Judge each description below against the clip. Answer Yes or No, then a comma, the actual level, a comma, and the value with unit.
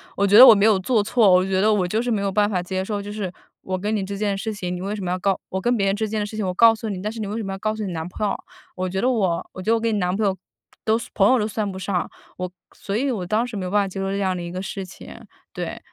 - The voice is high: Yes, high, 200 Hz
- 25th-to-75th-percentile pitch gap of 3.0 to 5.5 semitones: No, narrow, 2.5 semitones